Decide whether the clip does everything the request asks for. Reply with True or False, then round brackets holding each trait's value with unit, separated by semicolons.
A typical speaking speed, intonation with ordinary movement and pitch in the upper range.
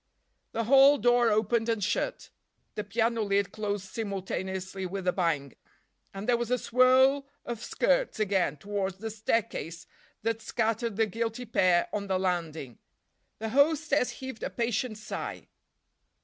True (145 wpm; 3.9 semitones; 220 Hz)